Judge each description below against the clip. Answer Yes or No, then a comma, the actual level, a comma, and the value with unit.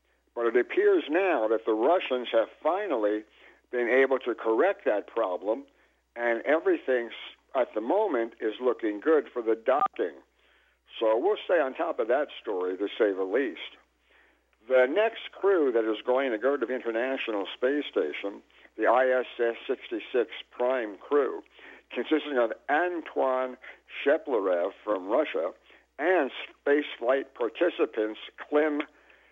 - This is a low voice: Yes, low, 130 Hz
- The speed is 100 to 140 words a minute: Yes, slow, 135 wpm